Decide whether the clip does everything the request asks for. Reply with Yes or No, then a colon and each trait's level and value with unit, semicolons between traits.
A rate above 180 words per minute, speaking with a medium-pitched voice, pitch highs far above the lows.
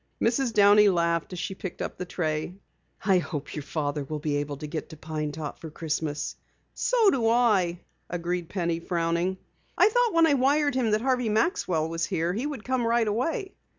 Yes: average, 195 wpm; medium, 180 Hz; wide, 7.0 semitones